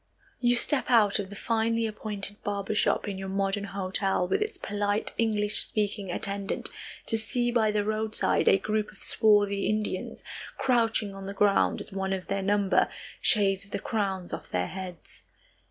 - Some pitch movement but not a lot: No, narrow, 1.8 semitones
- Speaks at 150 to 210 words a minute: Yes, average, 170 wpm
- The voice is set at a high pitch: Yes, high, 205 Hz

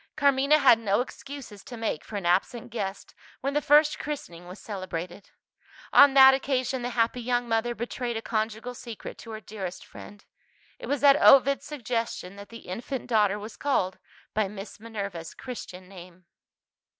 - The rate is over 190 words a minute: No, average, 165 wpm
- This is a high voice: Yes, high, 230 Hz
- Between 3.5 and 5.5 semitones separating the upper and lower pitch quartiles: Yes, average, 4.9 semitones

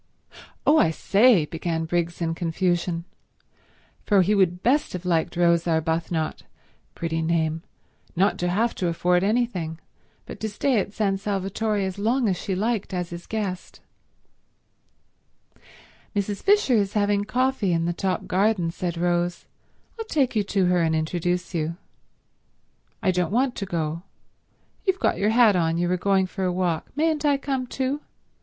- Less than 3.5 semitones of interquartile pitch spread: No, average, 3.9 semitones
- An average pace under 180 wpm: Yes, average, 160 wpm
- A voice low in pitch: No, medium, 185 Hz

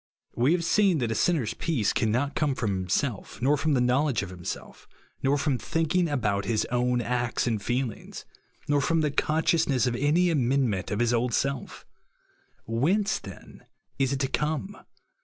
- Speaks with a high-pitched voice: No, low, 135 Hz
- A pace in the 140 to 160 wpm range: No, average, 175 wpm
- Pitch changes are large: No, average, 4.4 semitones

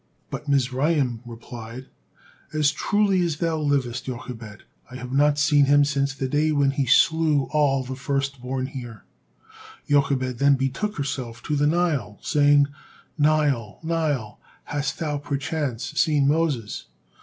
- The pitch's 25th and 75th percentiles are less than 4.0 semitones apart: Yes, narrow, 2.6 semitones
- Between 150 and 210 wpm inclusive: No, slow, 135 wpm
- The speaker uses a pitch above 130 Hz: Yes, medium, 140 Hz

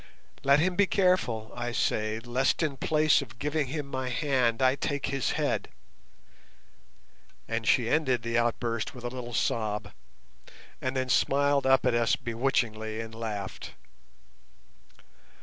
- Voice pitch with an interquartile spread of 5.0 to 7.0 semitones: No, average, 3.2 semitones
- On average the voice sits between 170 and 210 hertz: No, low, 125 Hz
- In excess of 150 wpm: No, average, 140 wpm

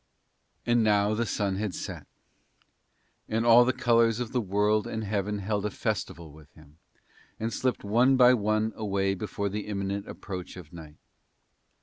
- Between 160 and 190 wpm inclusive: Yes, average, 165 wpm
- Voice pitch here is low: Yes, low, 105 Hz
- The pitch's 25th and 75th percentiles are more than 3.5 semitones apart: No, narrow, 2.6 semitones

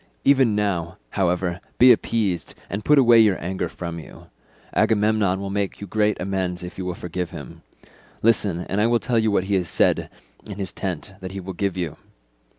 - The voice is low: Yes, very low, 95 Hz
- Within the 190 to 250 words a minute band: Yes, average, 195 wpm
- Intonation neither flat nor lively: Yes, average, 3.0 semitones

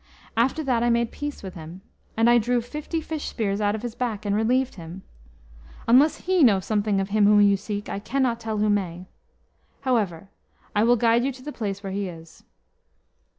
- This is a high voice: Yes, high, 220 Hz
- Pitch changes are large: No, average, 3.5 semitones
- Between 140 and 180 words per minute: No, average, 200 wpm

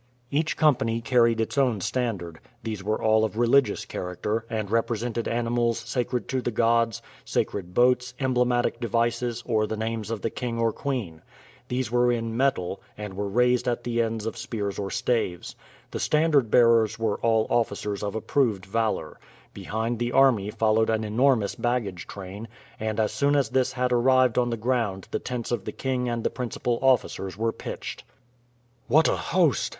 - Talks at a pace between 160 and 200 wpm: Yes, average, 175 wpm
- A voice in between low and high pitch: No, low, 115 Hz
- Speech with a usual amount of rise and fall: No, narrow, 2.3 semitones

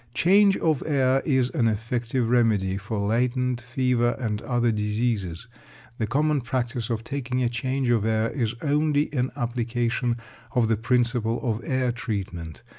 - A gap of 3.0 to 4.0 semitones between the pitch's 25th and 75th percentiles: No, narrow, 2.4 semitones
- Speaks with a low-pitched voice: Yes, low, 120 Hz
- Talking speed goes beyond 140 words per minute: Yes, average, 150 wpm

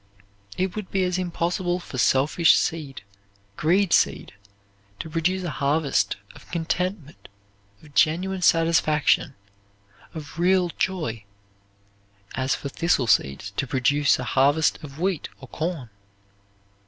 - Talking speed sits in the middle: No, slow, 120 wpm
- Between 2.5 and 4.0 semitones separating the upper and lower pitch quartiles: No, average, 4.5 semitones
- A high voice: No, medium, 160 Hz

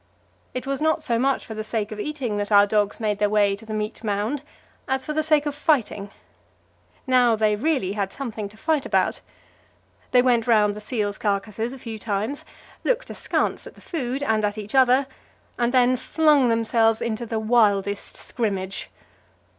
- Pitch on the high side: Yes, high, 225 Hz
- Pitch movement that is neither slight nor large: Yes, average, 4.0 semitones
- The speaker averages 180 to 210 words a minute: Yes, average, 185 wpm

